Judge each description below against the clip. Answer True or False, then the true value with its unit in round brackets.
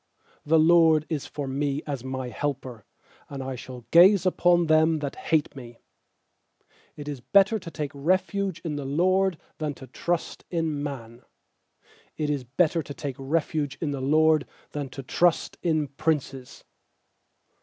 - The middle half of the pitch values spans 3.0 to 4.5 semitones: True (3.4 semitones)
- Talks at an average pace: True (155 wpm)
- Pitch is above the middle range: False (150 Hz)